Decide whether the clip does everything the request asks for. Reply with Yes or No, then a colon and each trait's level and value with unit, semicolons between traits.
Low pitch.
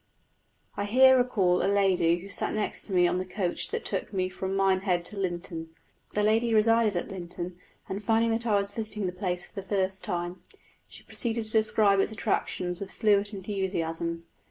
No: high, 195 Hz